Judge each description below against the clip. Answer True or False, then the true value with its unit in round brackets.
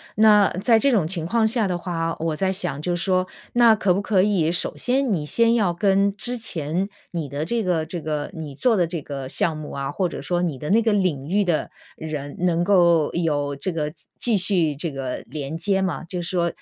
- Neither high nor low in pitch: True (175 Hz)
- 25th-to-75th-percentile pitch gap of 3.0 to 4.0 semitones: False (4.5 semitones)